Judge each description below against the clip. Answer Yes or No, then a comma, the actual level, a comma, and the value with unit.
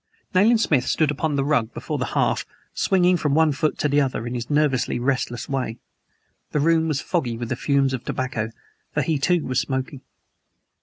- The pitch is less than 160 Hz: Yes, medium, 140 Hz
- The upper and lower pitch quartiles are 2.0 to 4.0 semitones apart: Yes, average, 3.5 semitones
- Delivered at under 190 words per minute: No, average, 195 wpm